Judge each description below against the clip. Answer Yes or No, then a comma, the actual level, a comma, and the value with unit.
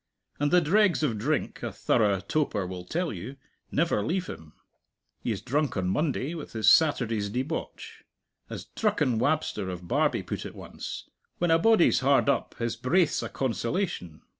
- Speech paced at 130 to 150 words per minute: No, average, 165 wpm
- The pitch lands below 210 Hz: Yes, low, 135 Hz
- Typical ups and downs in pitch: No, wide, 7.5 semitones